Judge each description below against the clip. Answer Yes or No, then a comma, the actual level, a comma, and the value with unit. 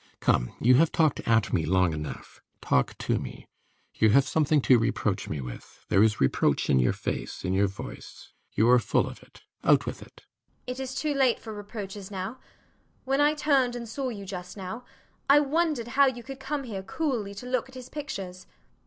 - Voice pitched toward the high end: Yes, high, 205 Hz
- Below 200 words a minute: No, fast, 205 wpm